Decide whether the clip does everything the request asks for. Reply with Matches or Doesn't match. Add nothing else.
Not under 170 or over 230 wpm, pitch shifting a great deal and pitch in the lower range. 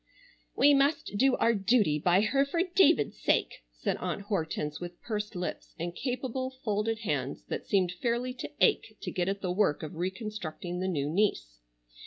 Doesn't match